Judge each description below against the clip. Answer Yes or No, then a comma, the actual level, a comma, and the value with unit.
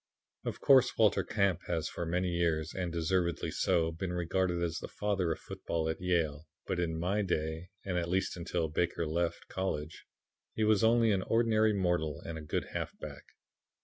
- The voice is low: Yes, very low, 85 Hz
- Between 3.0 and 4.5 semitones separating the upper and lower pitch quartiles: No, narrow, 2.6 semitones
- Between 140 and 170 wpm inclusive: No, average, 180 wpm